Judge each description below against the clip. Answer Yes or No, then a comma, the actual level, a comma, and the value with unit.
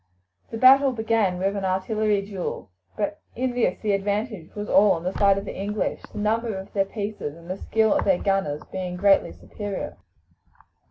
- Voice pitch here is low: No, high, 200 Hz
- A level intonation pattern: Yes, narrow, 2.3 semitones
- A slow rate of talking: No, average, 185 wpm